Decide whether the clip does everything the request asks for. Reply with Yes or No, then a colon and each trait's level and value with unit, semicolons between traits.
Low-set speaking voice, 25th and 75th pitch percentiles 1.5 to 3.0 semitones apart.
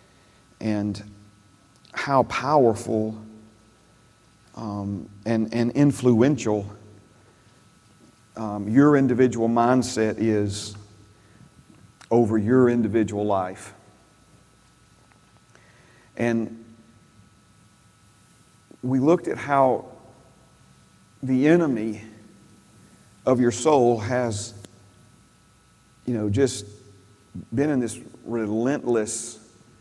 Yes: low, 110 Hz; narrow, 2.4 semitones